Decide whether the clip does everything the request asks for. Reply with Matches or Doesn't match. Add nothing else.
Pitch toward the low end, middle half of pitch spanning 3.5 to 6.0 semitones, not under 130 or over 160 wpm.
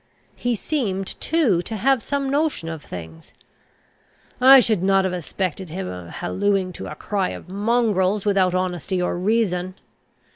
Doesn't match